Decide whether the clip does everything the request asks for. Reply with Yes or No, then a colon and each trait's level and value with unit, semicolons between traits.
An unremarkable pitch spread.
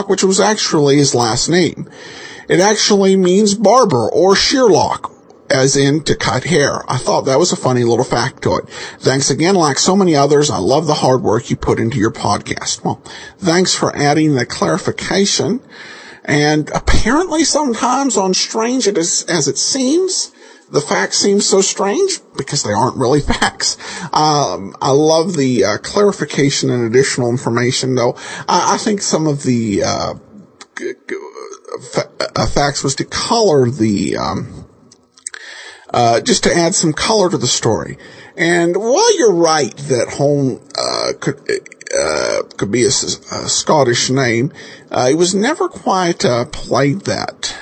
No: wide, 8.6 semitones